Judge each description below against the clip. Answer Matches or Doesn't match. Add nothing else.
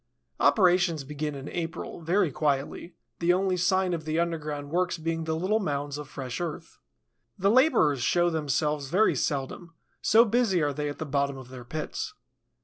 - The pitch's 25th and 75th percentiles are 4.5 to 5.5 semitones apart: Doesn't match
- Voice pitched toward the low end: Doesn't match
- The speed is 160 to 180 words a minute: Matches